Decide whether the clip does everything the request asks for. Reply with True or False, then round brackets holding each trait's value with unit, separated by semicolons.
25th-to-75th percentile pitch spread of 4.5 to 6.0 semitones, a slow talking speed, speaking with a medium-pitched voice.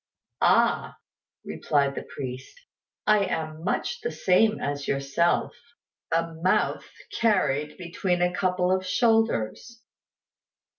True (5.3 semitones; 105 wpm; 180 Hz)